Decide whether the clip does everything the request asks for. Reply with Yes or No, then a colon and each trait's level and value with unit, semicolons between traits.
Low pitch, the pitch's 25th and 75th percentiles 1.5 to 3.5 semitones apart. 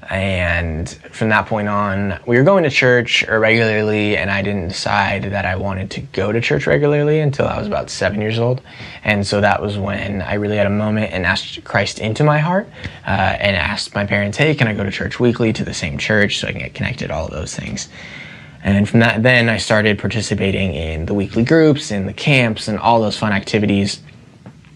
Yes: low, 105 Hz; average, 2.7 semitones